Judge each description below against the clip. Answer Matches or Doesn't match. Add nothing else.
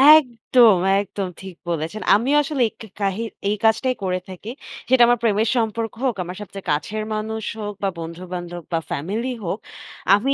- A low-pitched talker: Doesn't match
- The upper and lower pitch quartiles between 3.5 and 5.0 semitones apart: Matches